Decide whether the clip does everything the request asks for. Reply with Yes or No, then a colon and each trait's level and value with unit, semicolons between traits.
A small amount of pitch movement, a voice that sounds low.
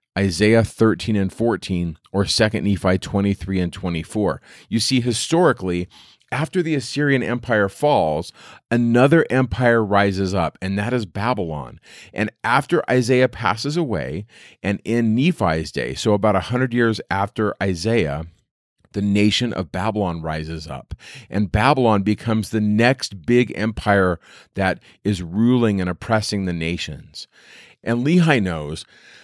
No: average, 4.0 semitones; low, 105 Hz